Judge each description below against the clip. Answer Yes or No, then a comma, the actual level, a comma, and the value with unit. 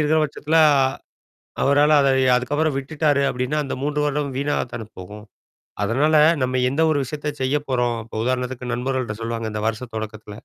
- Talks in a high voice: No, low, 130 Hz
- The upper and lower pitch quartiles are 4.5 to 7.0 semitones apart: No, average, 3.8 semitones